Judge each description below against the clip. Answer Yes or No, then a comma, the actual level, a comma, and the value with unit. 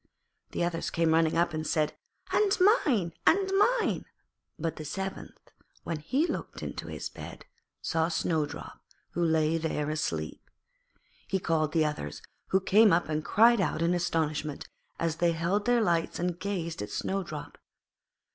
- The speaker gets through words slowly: No, average, 155 wpm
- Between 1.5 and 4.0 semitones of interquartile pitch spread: Yes, average, 3.5 semitones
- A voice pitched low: No, medium, 165 Hz